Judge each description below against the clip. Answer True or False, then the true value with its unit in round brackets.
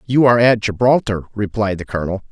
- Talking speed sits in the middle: True (180 wpm)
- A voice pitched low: True (105 Hz)